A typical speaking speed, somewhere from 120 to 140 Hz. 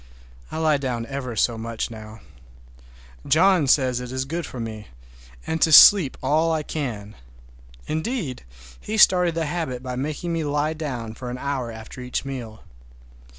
Yes: average, 160 wpm; low, 135 Hz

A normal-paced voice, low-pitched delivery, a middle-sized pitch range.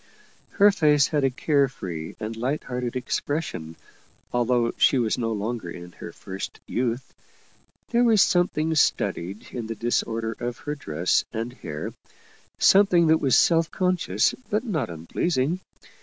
No: average, 155 wpm; low, 125 Hz; wide, 6.1 semitones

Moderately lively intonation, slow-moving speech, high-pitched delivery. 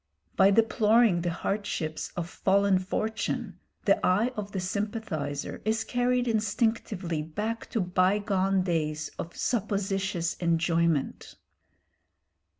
Yes: average, 4.1 semitones; slow, 105 wpm; high, 195 Hz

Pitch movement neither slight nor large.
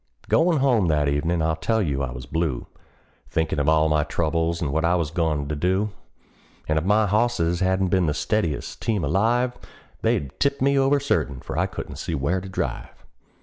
No: wide, 5.7 semitones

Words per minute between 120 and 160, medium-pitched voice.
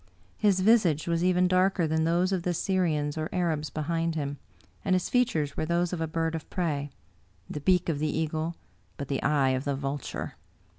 No: average, 195 wpm; medium, 165 Hz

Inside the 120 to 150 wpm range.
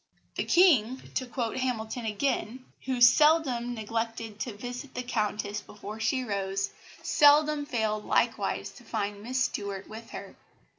Yes: average, 140 wpm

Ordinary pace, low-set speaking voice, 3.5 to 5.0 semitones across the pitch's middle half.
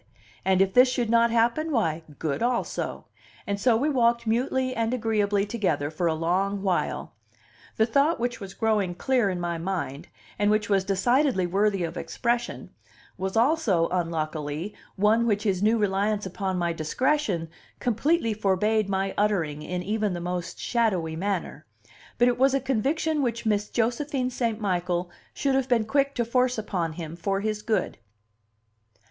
No: average, 165 wpm; high, 210 Hz; average, 4.7 semitones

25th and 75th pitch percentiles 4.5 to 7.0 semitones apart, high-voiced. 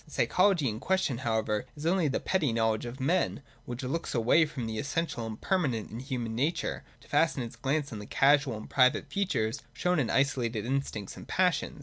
No: wide, 5.4 semitones; low, 130 Hz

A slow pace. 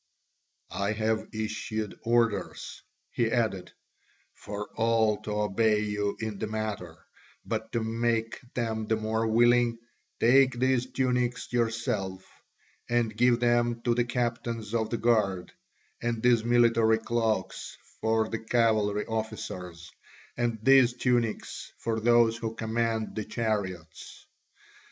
Yes: slow, 125 wpm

